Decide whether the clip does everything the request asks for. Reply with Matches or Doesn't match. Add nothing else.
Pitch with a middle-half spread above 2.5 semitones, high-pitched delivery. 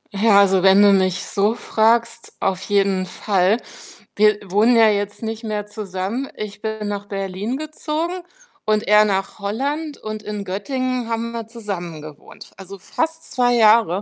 Matches